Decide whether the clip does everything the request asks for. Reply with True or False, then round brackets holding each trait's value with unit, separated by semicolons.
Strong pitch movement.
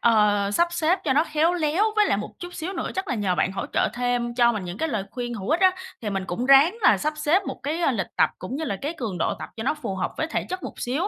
True (7.3 semitones)